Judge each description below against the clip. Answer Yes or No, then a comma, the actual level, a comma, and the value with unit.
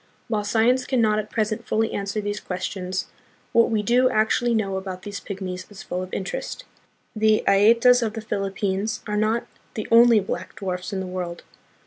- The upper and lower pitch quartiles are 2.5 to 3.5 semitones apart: Yes, average, 2.8 semitones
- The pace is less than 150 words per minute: No, average, 180 wpm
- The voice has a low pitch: No, high, 210 Hz